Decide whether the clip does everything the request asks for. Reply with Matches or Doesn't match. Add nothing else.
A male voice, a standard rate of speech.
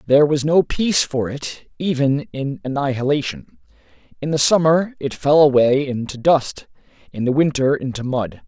Matches